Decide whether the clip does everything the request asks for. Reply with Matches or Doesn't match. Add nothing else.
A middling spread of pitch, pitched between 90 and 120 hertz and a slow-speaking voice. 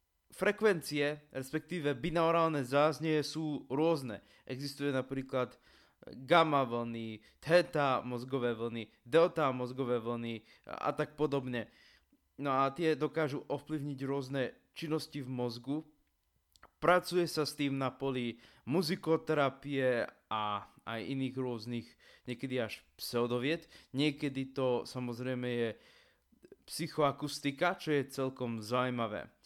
Doesn't match